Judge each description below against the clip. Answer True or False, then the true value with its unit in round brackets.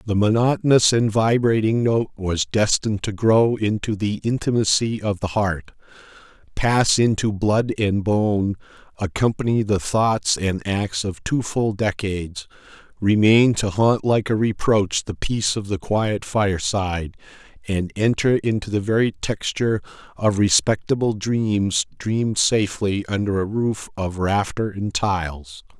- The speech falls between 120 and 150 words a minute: True (135 wpm)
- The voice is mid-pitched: False (105 Hz)